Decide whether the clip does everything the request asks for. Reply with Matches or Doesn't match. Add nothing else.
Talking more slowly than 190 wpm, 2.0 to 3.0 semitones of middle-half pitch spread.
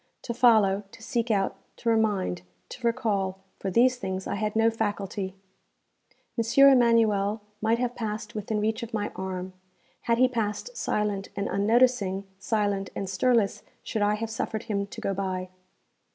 Matches